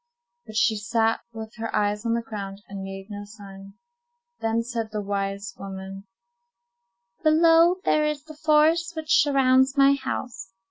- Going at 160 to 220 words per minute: No, average, 150 wpm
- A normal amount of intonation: No, wide, 6.1 semitones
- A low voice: No, high, 225 Hz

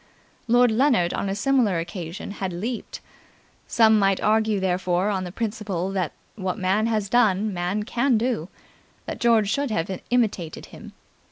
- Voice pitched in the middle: No, high, 205 Hz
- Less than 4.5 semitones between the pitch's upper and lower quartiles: Yes, average, 3.5 semitones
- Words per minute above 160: No, average, 155 wpm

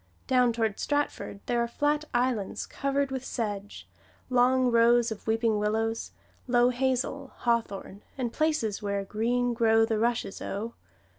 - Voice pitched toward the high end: Yes, high, 235 Hz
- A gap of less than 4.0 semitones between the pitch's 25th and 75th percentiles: Yes, narrow, 2.4 semitones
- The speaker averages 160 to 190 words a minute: No, average, 140 wpm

